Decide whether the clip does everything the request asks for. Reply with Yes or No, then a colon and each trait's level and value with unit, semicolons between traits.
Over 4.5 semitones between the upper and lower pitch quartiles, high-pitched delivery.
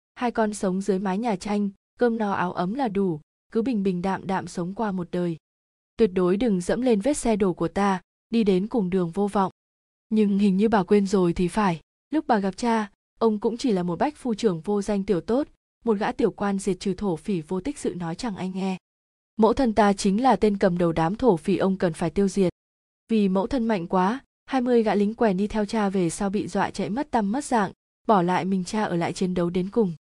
No: average, 3.3 semitones; high, 200 Hz